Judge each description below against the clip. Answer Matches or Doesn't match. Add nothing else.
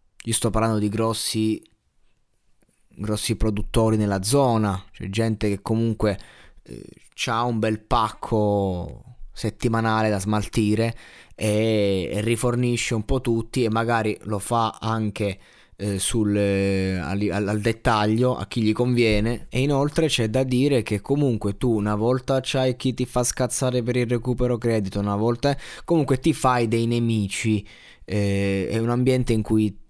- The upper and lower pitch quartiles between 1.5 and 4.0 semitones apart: Matches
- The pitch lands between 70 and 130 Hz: Matches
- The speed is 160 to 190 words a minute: Doesn't match